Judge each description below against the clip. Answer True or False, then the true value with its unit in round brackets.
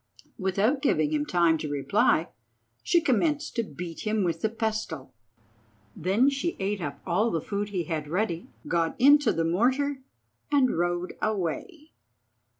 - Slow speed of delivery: False (150 wpm)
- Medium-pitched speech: False (205 Hz)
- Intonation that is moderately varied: False (7.7 semitones)